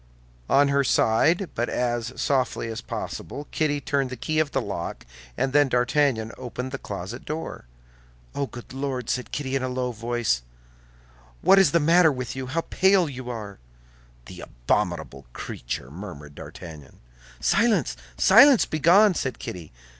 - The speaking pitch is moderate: No, low, 130 Hz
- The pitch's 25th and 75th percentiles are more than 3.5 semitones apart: Yes, average, 4.6 semitones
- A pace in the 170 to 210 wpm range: No, average, 155 wpm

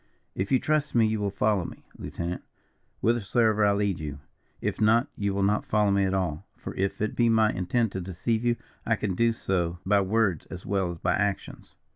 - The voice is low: Yes, low, 100 Hz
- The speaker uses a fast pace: Yes, fast, 210 wpm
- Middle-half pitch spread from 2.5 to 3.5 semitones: Yes, average, 2.9 semitones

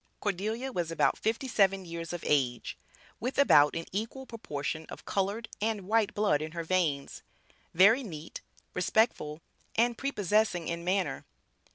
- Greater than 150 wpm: No, average, 145 wpm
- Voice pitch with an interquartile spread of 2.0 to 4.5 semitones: No, average, 5.1 semitones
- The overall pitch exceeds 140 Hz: Yes, high, 190 Hz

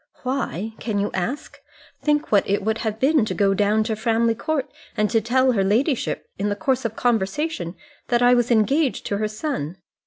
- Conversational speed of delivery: Yes, average, 195 wpm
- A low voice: No, high, 225 Hz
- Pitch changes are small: No, average, 4.0 semitones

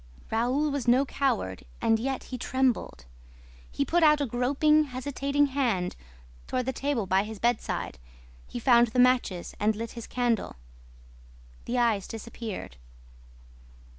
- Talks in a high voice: Yes, high, 245 Hz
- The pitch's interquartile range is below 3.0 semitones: No, average, 3.6 semitones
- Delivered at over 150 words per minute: No, slow, 135 wpm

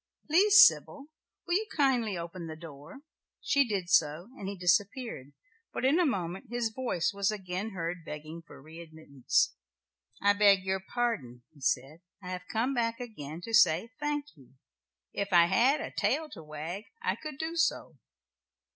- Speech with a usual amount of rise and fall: No, wide, 6.8 semitones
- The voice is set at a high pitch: Yes, high, 195 Hz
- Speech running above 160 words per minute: Yes, average, 170 wpm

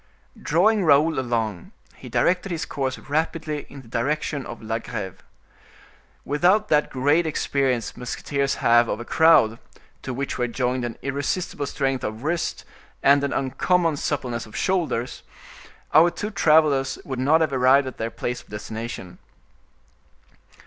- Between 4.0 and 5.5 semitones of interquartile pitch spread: Yes, average, 4.5 semitones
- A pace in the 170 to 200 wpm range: No, average, 145 wpm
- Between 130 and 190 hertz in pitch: Yes, medium, 140 Hz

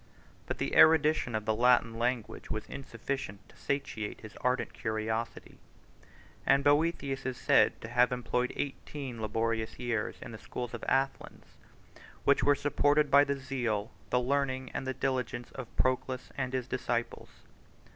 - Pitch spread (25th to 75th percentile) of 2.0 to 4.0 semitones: Yes, average, 3.0 semitones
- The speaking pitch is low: Yes, low, 125 Hz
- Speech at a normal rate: Yes, average, 155 wpm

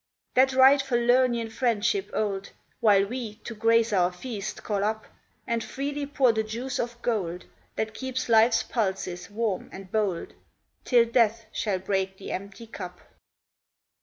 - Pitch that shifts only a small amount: No, average, 3.5 semitones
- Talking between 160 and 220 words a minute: No, average, 145 wpm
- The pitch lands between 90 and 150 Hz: No, high, 225 Hz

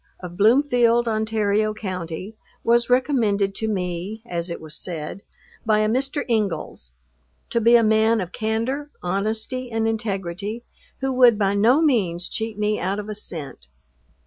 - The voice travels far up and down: No, average, 3.4 semitones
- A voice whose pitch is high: Yes, high, 215 Hz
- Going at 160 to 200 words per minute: No, average, 150 wpm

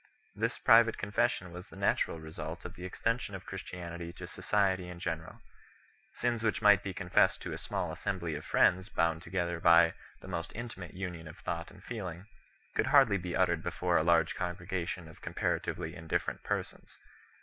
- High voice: No, very low, 90 Hz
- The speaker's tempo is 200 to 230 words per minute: No, average, 175 wpm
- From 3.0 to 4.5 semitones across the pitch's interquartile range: No, narrow, 2.5 semitones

